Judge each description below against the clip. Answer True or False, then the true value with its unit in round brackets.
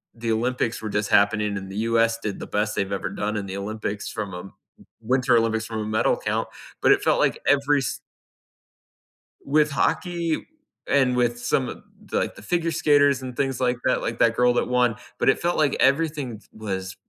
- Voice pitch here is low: True (115 Hz)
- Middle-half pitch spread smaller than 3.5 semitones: False (4.1 semitones)